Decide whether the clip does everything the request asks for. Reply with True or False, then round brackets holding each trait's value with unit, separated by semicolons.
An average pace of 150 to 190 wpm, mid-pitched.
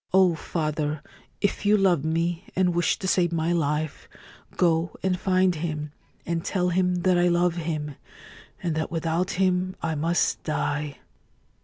True (155 wpm; 170 Hz)